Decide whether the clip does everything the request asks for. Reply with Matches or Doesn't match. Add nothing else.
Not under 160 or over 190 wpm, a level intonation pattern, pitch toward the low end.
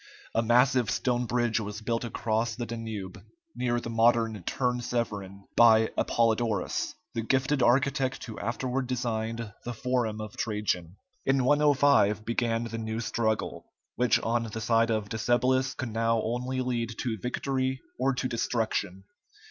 Doesn't match